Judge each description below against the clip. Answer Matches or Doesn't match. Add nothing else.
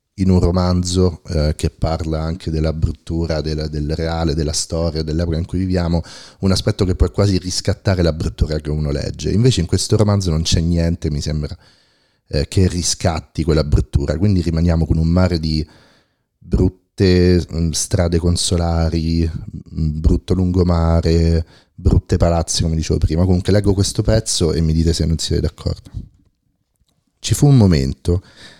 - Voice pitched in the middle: Doesn't match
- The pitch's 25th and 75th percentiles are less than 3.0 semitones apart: Matches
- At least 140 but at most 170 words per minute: Matches